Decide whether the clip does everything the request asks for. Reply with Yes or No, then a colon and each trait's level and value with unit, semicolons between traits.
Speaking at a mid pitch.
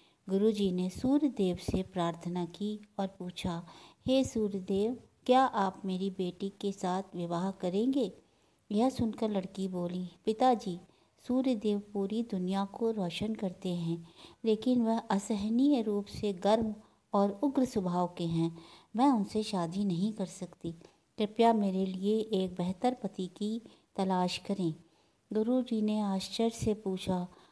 No: high, 200 Hz